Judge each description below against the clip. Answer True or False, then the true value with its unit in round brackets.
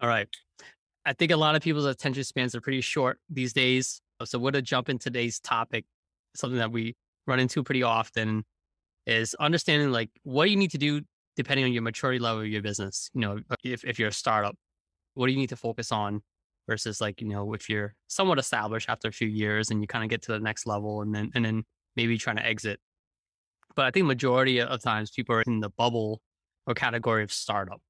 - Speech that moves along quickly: True (225 wpm)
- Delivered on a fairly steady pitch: False (3.3 semitones)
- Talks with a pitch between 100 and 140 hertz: True (115 Hz)